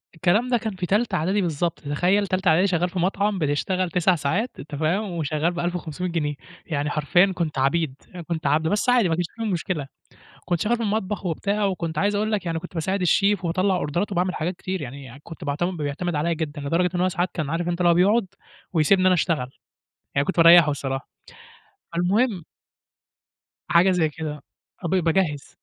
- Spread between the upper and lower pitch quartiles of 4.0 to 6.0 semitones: No, average, 3.4 semitones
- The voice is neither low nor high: Yes, medium, 175 Hz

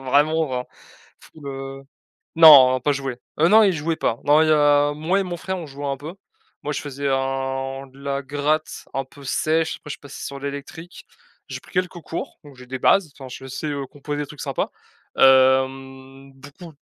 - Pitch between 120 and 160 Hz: Yes, medium, 140 Hz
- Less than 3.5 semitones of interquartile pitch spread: Yes, narrow, 2.6 semitones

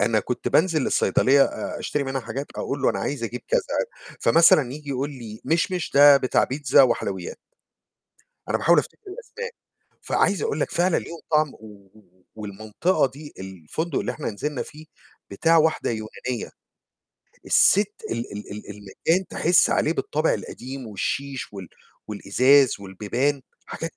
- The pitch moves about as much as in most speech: No, wide, 6.1 semitones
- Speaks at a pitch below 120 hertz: No, low, 135 Hz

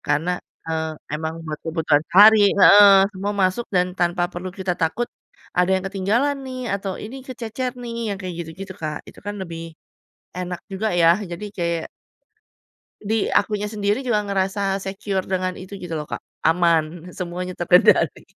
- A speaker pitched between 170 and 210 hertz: Yes, medium, 185 Hz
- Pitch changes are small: No, average, 3.2 semitones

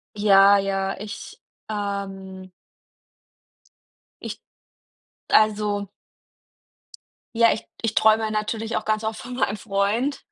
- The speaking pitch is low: No, high, 210 Hz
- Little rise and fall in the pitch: Yes, narrow, 1.7 semitones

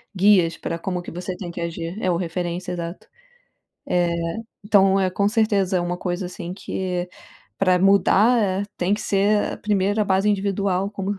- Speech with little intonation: Yes, narrow, 2.2 semitones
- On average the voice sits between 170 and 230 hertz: Yes, high, 190 Hz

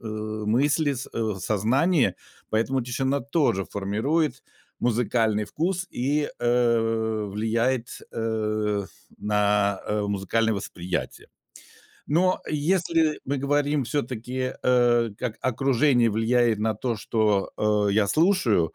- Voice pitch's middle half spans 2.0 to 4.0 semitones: No, average, 4.4 semitones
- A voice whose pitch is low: Yes, low, 115 Hz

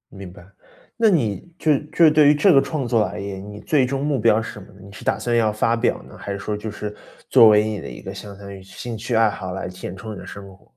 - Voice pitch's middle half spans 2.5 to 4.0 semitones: No, average, 4.4 semitones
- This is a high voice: No, low, 110 Hz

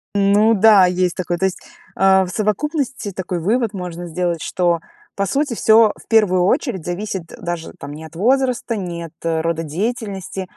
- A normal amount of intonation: Yes, average, 4.0 semitones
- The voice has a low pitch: No, high, 190 Hz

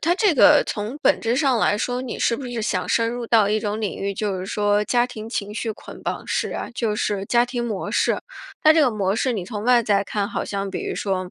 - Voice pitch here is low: No, high, 220 Hz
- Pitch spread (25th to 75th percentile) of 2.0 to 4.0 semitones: Yes, average, 3.2 semitones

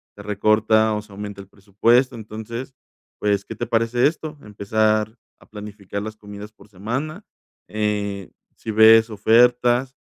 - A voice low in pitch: Yes, low, 110 Hz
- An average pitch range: No, narrow, 2.1 semitones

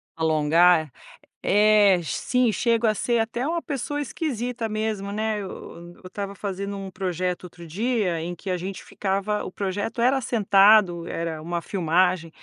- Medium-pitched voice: No, high, 195 Hz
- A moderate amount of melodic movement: Yes, average, 3.9 semitones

